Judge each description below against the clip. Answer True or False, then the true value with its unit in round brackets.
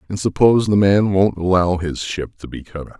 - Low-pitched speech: True (95 Hz)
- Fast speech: True (240 wpm)